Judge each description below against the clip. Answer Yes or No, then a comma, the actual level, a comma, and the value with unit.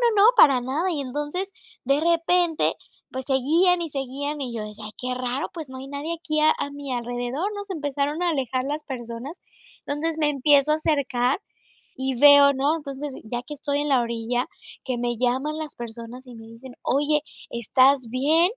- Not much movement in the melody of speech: No, average, 3.4 semitones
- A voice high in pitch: Yes, very high, 275 Hz